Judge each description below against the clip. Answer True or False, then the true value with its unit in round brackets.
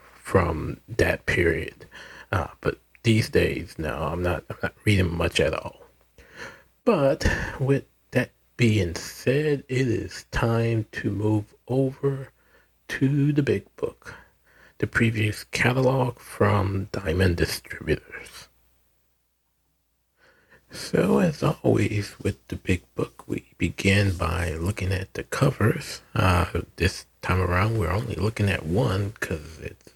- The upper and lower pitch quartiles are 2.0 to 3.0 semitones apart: False (4.9 semitones)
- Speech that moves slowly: True (125 wpm)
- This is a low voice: True (100 Hz)